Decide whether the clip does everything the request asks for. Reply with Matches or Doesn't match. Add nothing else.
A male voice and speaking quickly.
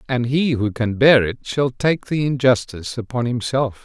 Doesn't match